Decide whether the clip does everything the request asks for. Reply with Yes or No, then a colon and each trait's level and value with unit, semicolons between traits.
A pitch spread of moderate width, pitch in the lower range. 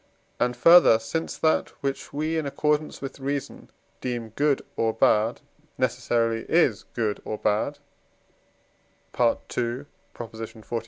Yes: average, 4.0 semitones; low, 125 Hz